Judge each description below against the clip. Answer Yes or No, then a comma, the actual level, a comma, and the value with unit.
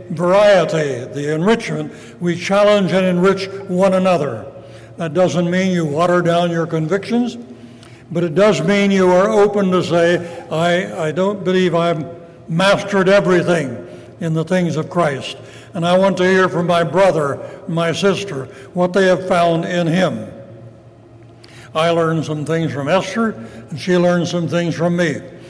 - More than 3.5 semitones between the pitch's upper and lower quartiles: No, average, 3.0 semitones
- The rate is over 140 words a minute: Yes, average, 160 wpm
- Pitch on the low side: No, medium, 175 Hz